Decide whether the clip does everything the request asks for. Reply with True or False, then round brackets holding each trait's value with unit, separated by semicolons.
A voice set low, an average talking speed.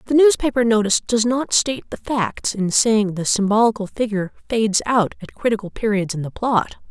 False (220 Hz; 185 wpm)